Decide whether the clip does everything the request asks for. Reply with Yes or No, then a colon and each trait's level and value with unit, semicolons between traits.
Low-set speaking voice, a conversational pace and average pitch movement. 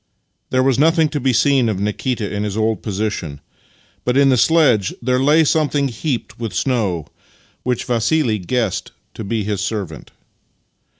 Yes: low, 120 Hz; average, 165 wpm; average, 4.5 semitones